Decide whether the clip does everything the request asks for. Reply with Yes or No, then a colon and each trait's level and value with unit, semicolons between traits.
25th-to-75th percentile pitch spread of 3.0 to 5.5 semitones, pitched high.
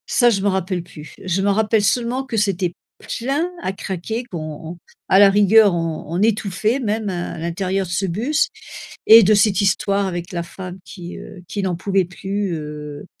Yes: average, 3.3 semitones; high, 195 Hz